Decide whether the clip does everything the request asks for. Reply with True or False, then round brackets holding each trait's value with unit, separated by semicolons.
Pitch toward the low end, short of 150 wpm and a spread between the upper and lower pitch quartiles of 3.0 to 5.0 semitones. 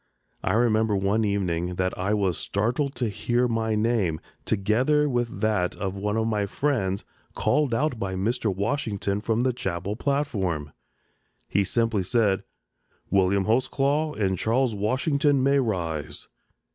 True (110 Hz; 140 wpm; 4.2 semitones)